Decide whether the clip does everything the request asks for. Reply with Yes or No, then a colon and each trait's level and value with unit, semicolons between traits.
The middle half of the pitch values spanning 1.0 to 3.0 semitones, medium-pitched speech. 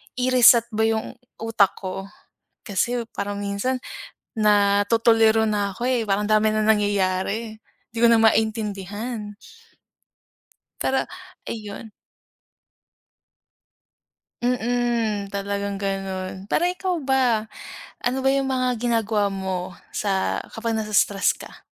No: average, 2.7 semitones; high, 215 Hz